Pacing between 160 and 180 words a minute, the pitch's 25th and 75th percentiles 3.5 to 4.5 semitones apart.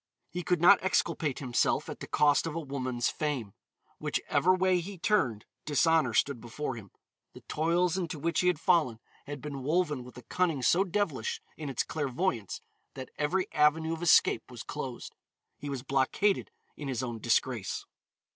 No: average, 175 wpm; average, 5.3 semitones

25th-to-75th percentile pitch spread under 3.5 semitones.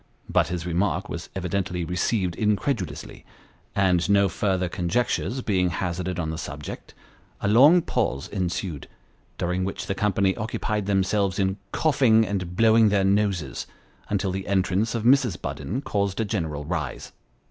Yes: average, 2.9 semitones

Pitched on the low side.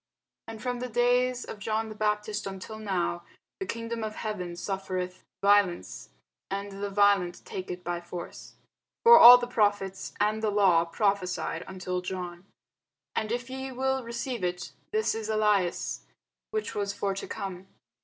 No: high, 205 Hz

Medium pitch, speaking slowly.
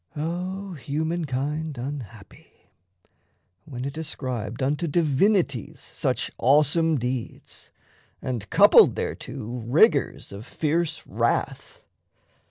Yes: medium, 145 Hz; slow, 85 wpm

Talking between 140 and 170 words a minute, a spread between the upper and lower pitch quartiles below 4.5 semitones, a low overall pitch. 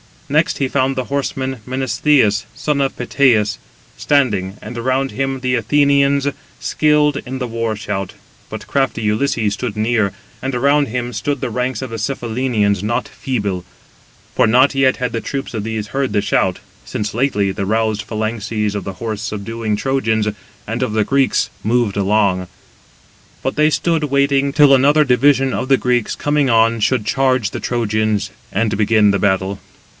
Yes: average, 165 wpm; average, 4.1 semitones; low, 120 Hz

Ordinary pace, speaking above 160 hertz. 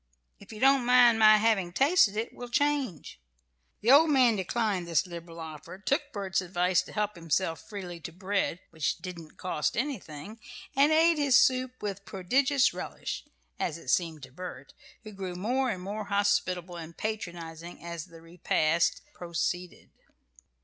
Yes: average, 155 wpm; high, 190 Hz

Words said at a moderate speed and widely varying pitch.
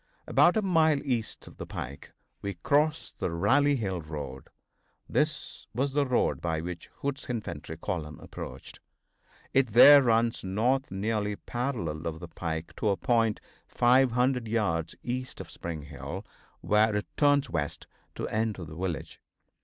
Yes: average, 150 wpm; wide, 7.5 semitones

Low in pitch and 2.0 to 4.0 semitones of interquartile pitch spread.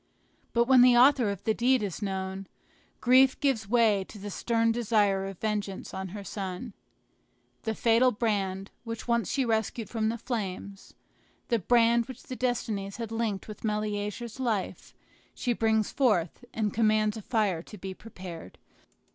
No: high, 220 Hz; average, 3.0 semitones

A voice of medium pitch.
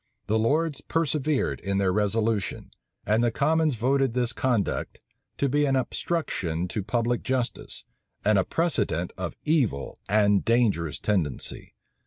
No: low, 115 Hz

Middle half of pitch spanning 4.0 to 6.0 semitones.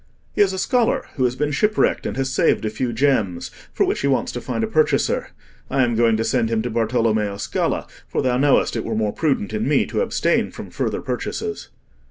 Yes: average, 4.5 semitones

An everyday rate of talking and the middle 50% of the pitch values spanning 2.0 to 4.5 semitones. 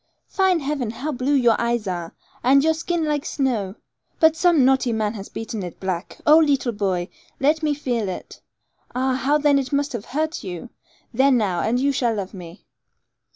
No: average, 190 wpm; wide, 5.5 semitones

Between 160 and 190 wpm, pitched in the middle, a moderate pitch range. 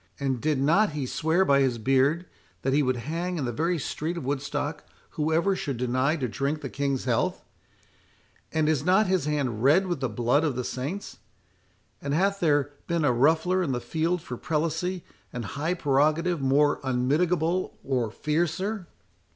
Yes: average, 165 wpm; medium, 145 Hz; average, 4.2 semitones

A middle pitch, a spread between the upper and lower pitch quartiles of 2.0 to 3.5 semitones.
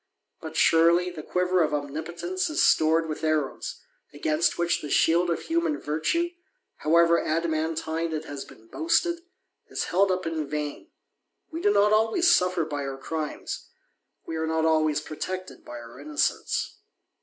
Yes: medium, 165 Hz; average, 3.1 semitones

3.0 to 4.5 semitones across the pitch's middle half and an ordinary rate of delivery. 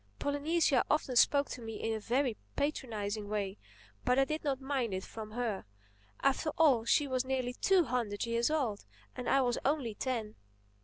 Yes: average, 4.1 semitones; average, 175 wpm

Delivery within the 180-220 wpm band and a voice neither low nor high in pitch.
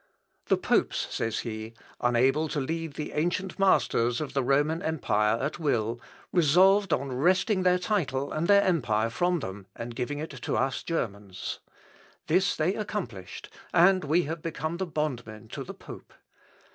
No: average, 155 wpm; medium, 150 Hz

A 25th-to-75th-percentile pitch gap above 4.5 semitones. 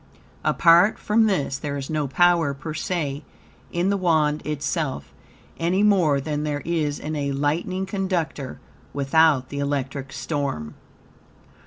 No: average, 3.6 semitones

